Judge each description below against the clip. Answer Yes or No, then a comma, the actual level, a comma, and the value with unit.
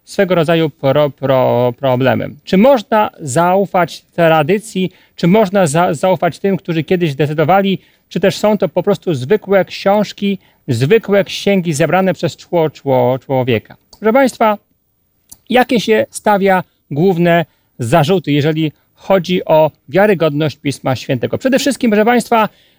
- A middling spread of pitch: Yes, average, 4.3 semitones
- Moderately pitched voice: Yes, medium, 180 Hz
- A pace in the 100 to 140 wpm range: Yes, average, 125 wpm